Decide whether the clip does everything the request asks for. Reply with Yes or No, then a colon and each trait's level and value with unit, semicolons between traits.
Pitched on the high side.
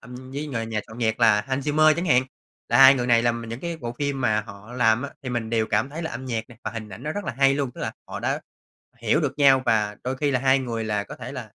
No: low, 125 Hz